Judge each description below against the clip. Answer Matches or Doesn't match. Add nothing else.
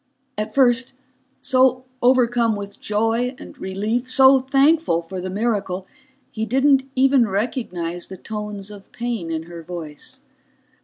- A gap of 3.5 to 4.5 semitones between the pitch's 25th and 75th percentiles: Doesn't match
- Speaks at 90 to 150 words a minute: Matches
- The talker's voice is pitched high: Matches